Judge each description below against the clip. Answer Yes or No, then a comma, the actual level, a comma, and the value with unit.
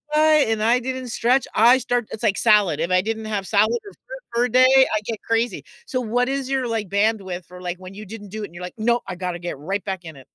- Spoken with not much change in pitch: No, average, 4.4 semitones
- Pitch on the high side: Yes, high, 220 Hz